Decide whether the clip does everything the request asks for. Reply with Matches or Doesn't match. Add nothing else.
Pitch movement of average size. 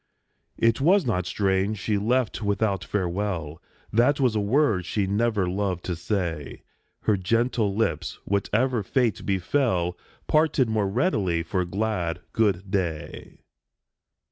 Matches